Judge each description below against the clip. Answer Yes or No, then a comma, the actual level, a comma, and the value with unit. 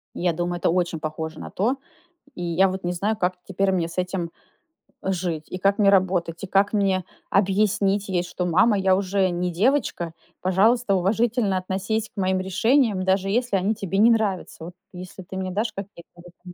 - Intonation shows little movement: Yes, narrow, 2.2 semitones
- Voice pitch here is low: No, high, 190 Hz